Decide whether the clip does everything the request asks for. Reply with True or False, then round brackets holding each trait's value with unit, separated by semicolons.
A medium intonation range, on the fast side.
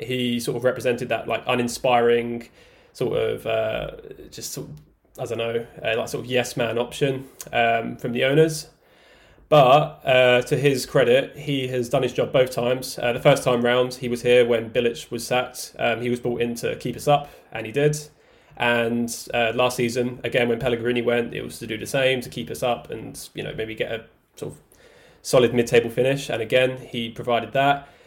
False (2.3 semitones; 210 wpm)